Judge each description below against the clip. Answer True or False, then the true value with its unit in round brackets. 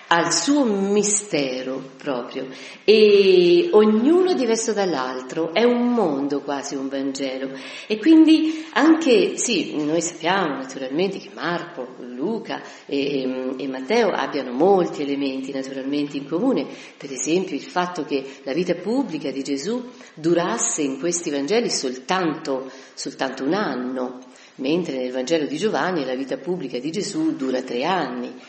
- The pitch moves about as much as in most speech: False (8.2 semitones)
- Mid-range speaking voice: True (155 Hz)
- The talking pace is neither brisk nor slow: True (135 wpm)